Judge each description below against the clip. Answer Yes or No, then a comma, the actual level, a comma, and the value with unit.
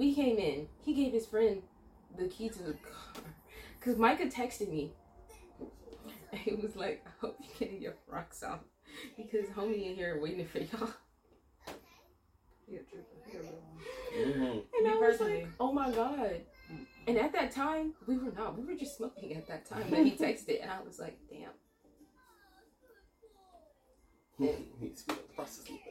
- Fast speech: No, average, 155 wpm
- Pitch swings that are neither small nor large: No, wide, 6.3 semitones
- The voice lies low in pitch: No, high, 245 Hz